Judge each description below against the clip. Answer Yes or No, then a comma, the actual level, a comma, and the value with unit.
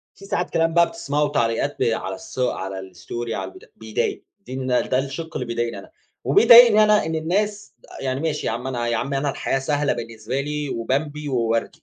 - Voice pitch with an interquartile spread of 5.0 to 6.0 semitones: Yes, wide, 5.4 semitones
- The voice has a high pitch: No, low, 135 Hz